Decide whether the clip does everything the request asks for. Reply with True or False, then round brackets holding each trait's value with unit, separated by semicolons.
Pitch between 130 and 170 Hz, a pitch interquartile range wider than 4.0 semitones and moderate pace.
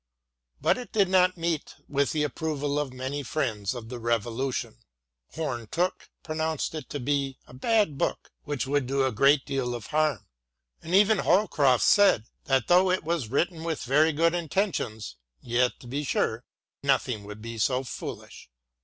True (140 Hz; 4.7 semitones; 175 wpm)